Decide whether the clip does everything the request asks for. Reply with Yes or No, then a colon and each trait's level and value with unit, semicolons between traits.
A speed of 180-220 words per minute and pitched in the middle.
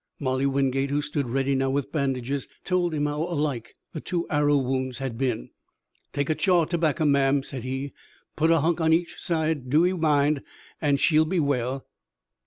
Yes: average, 185 wpm; medium, 145 Hz